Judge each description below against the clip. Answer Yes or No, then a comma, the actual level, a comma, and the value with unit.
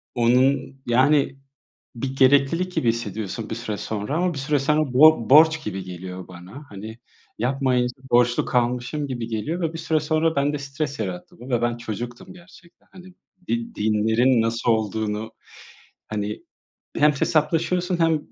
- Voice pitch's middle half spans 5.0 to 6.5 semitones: Yes, average, 5.3 semitones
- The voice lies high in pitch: No, low, 130 Hz